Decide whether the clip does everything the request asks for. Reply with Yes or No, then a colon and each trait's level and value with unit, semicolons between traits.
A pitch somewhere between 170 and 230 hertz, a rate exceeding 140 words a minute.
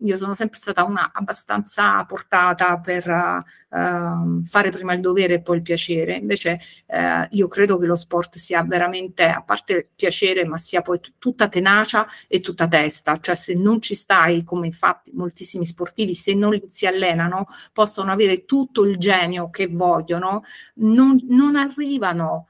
Yes: medium, 185 Hz; average, 165 wpm